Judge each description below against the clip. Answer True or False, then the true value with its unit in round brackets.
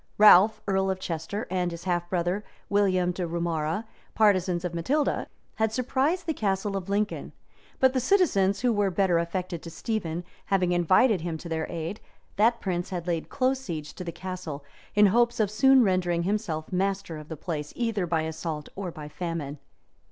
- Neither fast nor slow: True (175 wpm)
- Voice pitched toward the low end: False (185 Hz)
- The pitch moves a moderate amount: True (3.8 semitones)